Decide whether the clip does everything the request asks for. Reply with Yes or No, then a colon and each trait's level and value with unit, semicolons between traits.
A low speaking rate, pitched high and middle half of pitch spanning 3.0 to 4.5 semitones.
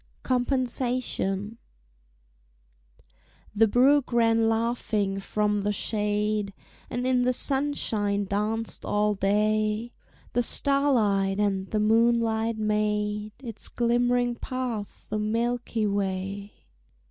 No: slow, 95 wpm; high, 215 Hz; narrow, 2.6 semitones